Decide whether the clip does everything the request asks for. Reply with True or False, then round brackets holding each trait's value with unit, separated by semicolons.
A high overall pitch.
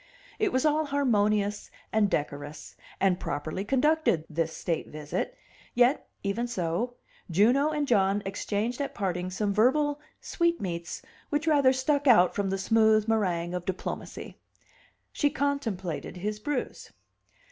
True (215 Hz)